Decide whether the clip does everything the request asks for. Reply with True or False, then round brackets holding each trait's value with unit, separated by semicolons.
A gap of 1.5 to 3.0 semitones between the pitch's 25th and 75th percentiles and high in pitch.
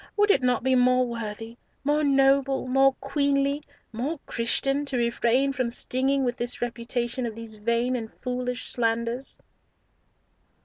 True (2.6 semitones; 250 Hz)